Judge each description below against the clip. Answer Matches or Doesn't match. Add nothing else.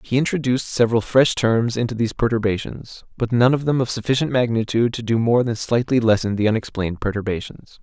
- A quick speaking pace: Doesn't match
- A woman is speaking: Doesn't match